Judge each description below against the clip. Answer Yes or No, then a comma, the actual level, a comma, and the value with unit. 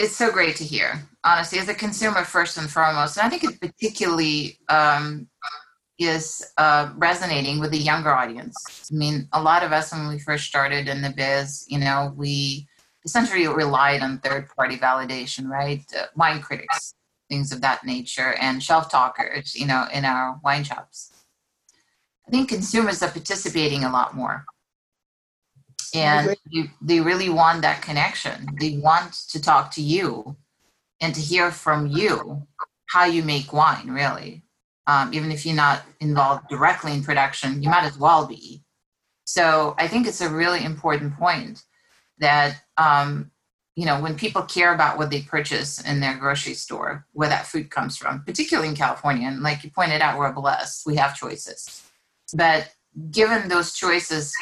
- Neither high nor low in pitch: Yes, medium, 150 Hz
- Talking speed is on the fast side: No, average, 170 wpm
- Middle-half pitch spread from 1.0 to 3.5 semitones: Yes, average, 3.0 semitones